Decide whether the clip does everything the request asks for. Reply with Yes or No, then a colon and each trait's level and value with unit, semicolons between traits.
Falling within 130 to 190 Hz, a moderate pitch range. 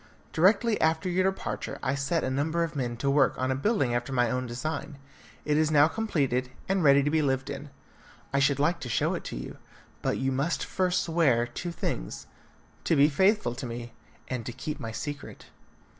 Yes: medium, 140 Hz; average, 4.2 semitones